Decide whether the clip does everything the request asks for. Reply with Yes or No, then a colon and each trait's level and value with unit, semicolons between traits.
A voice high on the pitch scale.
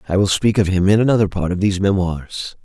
No: very low, 95 Hz